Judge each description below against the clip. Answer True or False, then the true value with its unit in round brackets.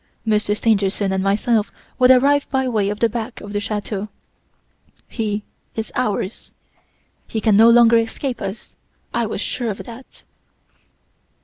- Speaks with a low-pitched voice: False (220 Hz)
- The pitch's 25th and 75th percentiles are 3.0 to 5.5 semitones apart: False (2.5 semitones)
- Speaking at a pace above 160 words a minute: False (145 wpm)